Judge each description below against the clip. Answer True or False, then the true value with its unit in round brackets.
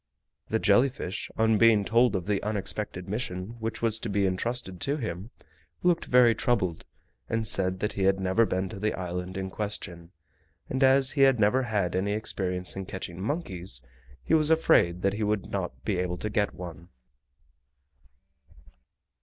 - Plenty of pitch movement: False (3.8 semitones)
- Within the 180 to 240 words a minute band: False (170 wpm)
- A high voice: False (105 Hz)